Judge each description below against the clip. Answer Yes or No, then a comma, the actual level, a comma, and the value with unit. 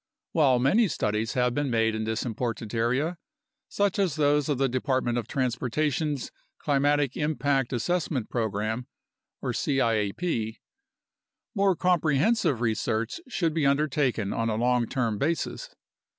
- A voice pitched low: Yes, low, 130 Hz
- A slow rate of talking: Yes, slow, 125 wpm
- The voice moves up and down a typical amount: Yes, average, 4.8 semitones